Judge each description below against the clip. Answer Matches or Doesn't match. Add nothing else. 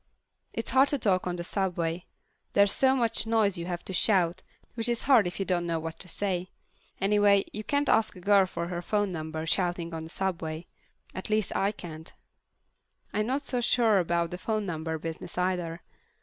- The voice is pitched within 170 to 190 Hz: Matches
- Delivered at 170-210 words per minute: Matches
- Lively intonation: Doesn't match